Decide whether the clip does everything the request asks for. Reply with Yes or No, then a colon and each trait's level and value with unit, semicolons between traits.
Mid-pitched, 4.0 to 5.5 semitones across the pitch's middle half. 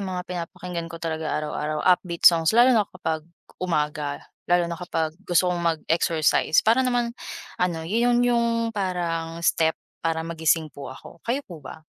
No: medium, 170 Hz; average, 2.7 semitones